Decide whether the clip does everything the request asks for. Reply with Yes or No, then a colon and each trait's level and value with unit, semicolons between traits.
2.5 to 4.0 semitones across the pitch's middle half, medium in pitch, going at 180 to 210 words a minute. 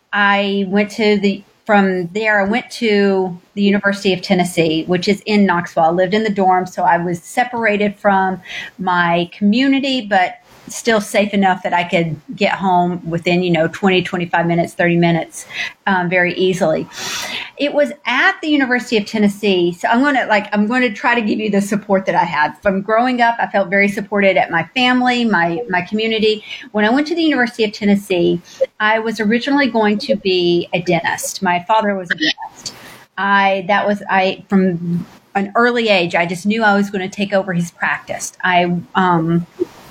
No: average, 3.4 semitones; high, 200 Hz; average, 190 wpm